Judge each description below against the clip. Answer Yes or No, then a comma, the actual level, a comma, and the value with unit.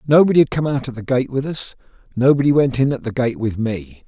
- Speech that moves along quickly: Yes, fast, 250 wpm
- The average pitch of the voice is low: Yes, low, 130 Hz